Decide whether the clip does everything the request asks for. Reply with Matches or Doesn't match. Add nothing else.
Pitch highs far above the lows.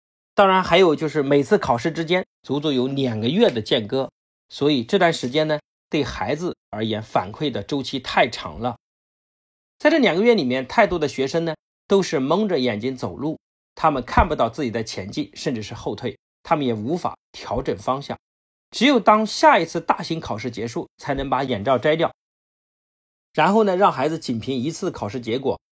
Matches